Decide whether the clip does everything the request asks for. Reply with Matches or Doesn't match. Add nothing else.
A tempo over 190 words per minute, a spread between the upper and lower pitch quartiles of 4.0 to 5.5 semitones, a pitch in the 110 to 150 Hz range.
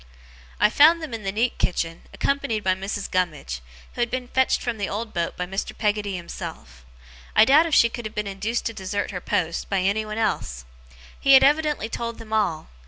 Doesn't match